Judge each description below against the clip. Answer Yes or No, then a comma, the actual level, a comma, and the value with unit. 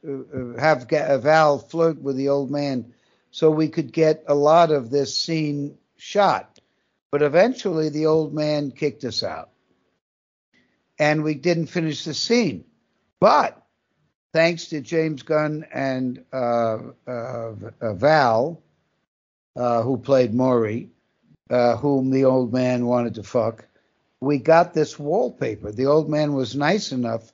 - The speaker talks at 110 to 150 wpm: Yes, slow, 135 wpm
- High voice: No, medium, 140 Hz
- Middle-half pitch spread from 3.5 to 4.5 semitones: Yes, average, 3.8 semitones